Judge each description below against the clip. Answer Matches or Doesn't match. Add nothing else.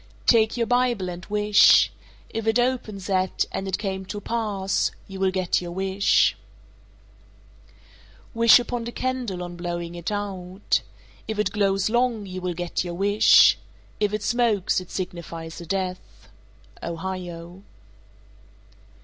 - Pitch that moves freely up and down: Doesn't match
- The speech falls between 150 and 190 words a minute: Doesn't match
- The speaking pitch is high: Matches